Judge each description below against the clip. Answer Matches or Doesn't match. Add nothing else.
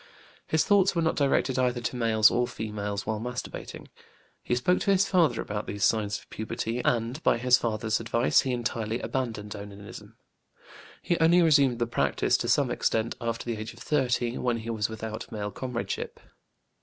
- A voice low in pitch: Matches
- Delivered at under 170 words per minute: Doesn't match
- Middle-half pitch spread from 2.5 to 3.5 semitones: Matches